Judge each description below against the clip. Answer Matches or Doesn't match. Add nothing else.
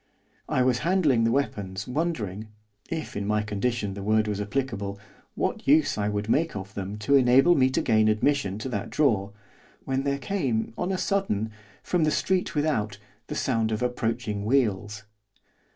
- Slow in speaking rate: Doesn't match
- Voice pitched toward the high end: Doesn't match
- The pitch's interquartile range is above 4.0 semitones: Matches